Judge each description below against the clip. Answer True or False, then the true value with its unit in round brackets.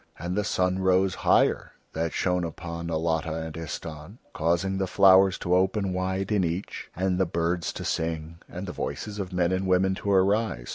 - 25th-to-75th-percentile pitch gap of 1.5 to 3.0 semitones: True (2.4 semitones)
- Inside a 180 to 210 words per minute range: True (185 wpm)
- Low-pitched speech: True (90 Hz)